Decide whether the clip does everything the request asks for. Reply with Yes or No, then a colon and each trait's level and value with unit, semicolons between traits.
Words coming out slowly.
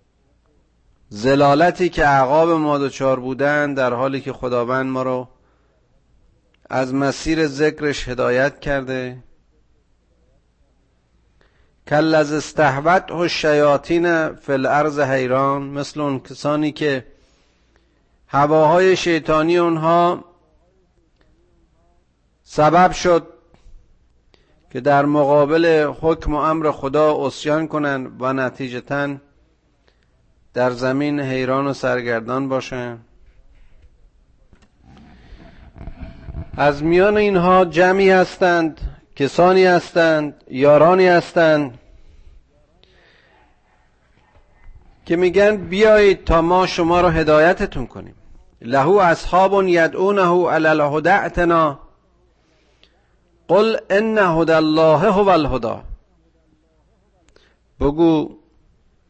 Yes: slow, 80 wpm